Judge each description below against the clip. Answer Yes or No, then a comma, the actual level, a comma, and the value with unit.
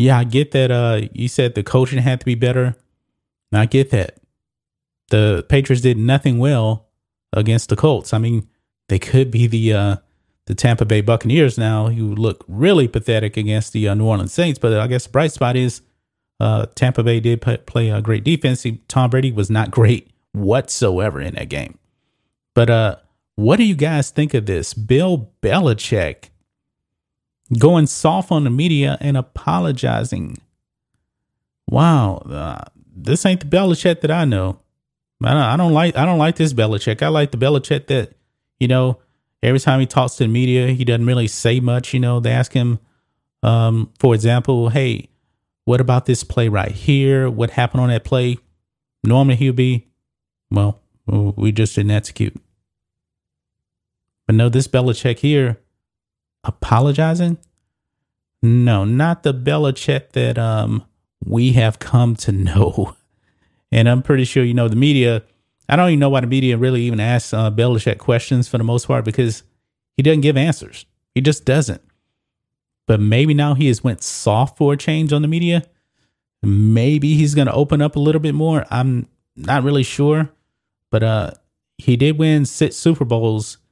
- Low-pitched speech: Yes, low, 125 Hz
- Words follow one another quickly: No, average, 170 wpm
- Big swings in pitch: No, average, 3.9 semitones